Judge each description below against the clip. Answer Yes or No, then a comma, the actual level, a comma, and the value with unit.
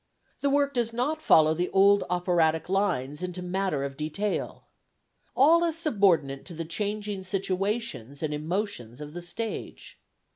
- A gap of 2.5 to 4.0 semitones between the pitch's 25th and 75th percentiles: No, average, 5.1 semitones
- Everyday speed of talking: Yes, average, 145 wpm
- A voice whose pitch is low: No, medium, 185 Hz